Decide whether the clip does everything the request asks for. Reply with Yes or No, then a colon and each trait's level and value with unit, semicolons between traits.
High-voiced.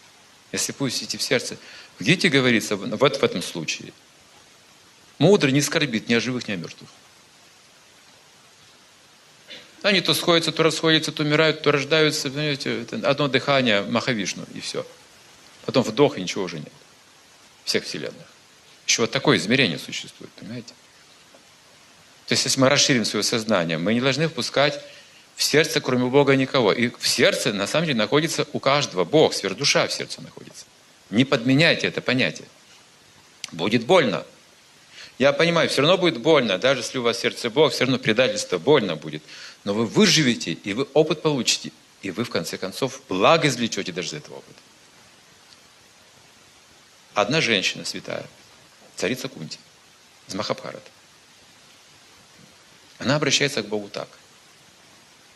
No: medium, 140 Hz